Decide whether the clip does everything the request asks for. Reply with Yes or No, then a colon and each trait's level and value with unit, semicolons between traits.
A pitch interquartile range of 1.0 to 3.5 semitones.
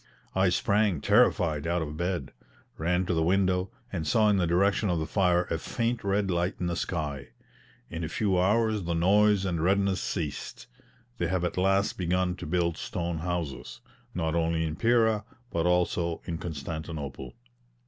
Yes: average, 3.0 semitones